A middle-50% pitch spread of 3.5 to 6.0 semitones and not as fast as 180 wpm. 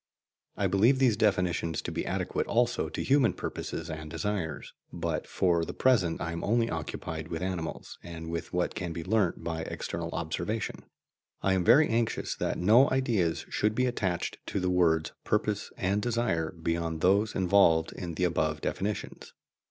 Yes: average, 4.5 semitones; average, 170 wpm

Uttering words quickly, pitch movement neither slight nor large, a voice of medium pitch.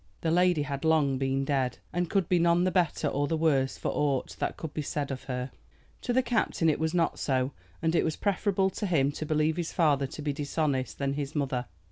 Yes: fast, 230 wpm; average, 3.7 semitones; medium, 155 Hz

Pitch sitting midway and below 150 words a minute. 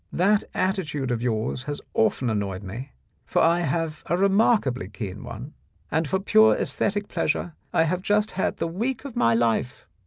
No: medium, 160 Hz; average, 175 wpm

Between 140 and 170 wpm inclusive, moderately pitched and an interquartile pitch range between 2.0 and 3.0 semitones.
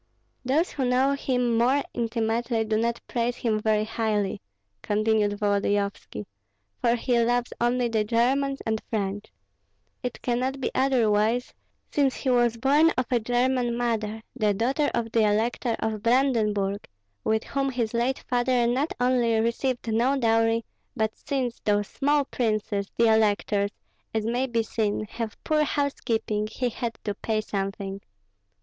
No: average, 145 wpm; high, 230 Hz; narrow, 2.6 semitones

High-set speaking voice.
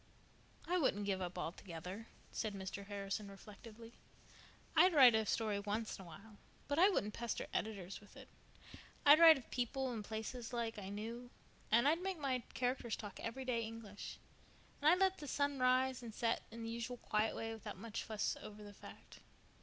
Yes: high, 225 Hz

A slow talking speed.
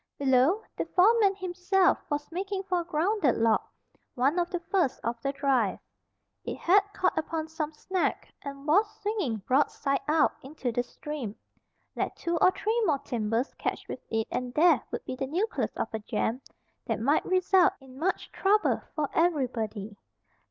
No: average, 165 wpm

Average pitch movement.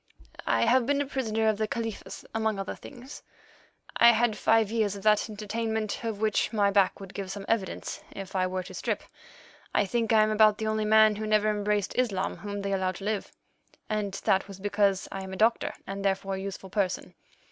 No: narrow, 2.0 semitones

